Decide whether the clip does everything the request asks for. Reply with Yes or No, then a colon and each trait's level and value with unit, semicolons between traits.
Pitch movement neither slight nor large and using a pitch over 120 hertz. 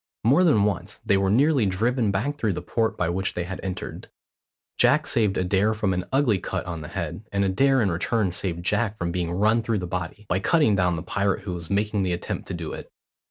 No: average, 3.6 semitones; low, 100 Hz